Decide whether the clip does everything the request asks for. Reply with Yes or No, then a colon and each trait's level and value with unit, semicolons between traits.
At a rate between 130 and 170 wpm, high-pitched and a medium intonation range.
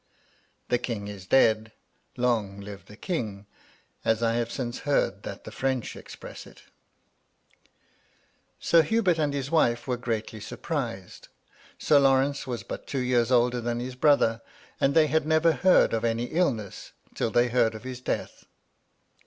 No: average, 165 wpm; low, 125 Hz; average, 3.8 semitones